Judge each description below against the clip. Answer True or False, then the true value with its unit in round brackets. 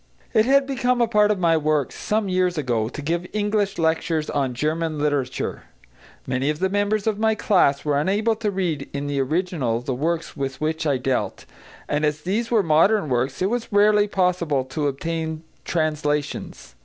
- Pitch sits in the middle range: True (160 Hz)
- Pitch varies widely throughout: True (6.0 semitones)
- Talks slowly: False (180 wpm)